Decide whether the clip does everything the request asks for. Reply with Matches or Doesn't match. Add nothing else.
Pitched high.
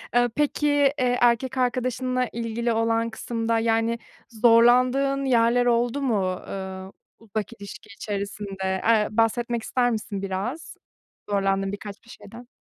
Matches